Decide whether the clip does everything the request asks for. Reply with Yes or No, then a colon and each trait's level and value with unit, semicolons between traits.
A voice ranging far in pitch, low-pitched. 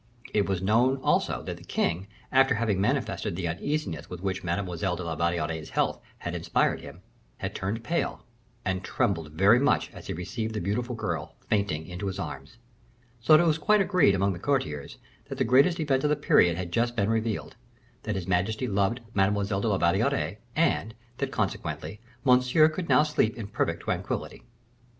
Yes: wide, 5.8 semitones; low, 100 Hz